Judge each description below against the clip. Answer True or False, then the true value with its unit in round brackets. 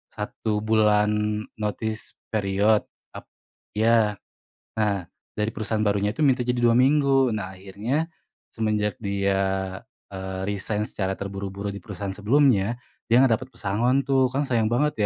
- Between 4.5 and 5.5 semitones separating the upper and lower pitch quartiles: False (3.4 semitones)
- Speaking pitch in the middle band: False (105 Hz)